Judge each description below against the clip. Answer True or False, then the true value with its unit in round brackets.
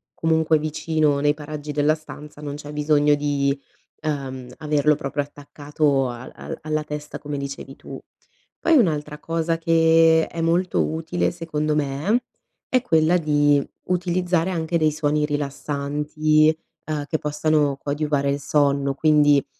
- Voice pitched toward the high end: False (150 Hz)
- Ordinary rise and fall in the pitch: False (1.7 semitones)